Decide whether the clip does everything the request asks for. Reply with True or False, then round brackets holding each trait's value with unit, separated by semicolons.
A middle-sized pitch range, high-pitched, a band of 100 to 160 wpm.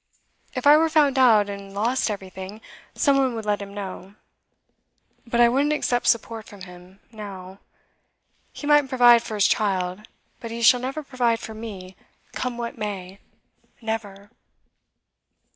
True (3.9 semitones; 220 Hz; 150 wpm)